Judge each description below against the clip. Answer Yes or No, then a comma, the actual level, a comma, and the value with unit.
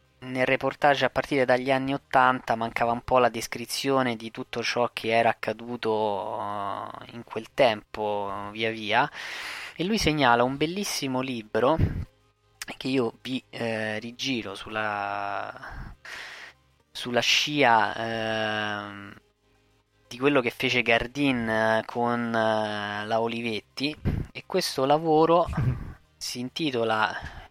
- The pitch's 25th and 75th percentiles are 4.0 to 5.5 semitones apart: No, average, 3.5 semitones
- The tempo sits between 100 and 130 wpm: Yes, slow, 115 wpm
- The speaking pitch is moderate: No, low, 115 Hz